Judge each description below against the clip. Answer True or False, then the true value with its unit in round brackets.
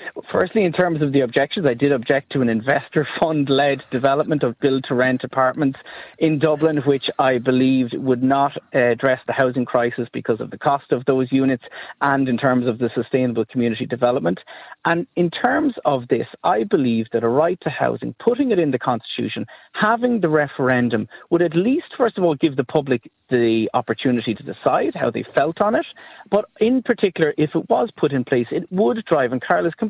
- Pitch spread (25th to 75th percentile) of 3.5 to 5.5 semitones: True (5.0 semitones)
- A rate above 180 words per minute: True (190 wpm)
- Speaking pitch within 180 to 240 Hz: False (140 Hz)